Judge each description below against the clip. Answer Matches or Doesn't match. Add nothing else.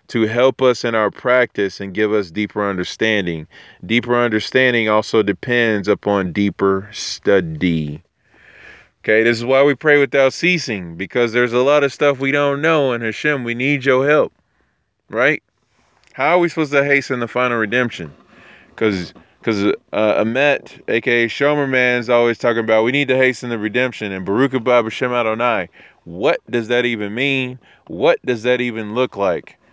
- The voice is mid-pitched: Doesn't match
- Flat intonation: Doesn't match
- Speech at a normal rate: Matches